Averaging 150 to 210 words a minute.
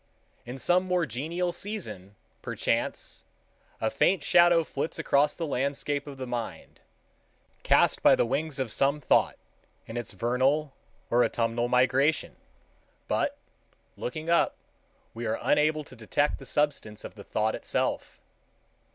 No: slow, 135 wpm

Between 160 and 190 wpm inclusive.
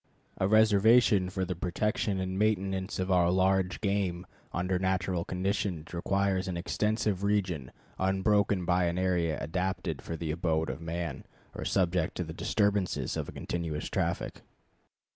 No: average, 145 wpm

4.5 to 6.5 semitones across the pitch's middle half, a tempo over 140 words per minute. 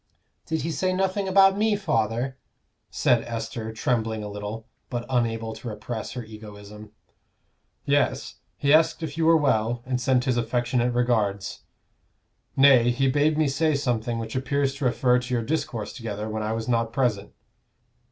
No: average, 4.1 semitones; average, 160 wpm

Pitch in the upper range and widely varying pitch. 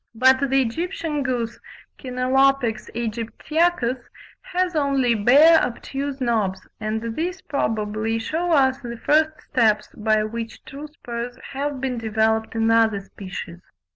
No: very high, 250 Hz; average, 4.0 semitones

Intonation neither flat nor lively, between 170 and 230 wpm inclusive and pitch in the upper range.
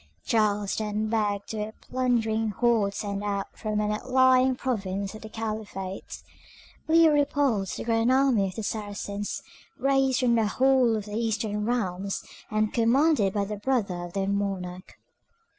No: average, 3.4 semitones; average, 150 wpm; high, 215 Hz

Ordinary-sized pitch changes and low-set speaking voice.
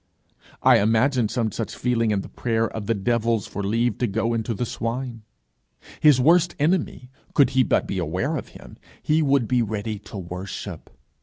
Yes: average, 3.3 semitones; low, 115 Hz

